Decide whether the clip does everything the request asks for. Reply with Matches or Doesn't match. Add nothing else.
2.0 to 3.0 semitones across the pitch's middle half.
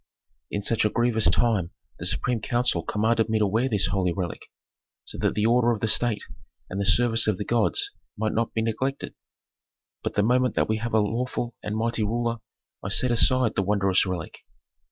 Matches